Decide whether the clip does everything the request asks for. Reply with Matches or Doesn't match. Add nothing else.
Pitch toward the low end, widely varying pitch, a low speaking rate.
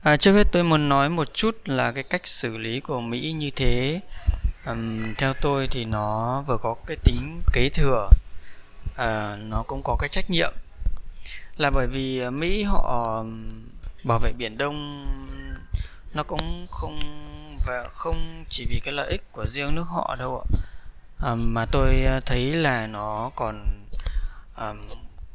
Matches